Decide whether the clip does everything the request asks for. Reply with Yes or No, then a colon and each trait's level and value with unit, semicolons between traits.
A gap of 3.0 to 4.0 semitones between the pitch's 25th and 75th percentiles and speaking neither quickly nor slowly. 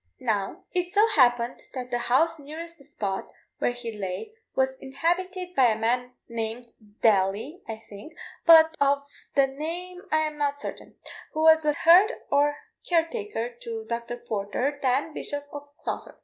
No: wide, 5.6 semitones; average, 165 wpm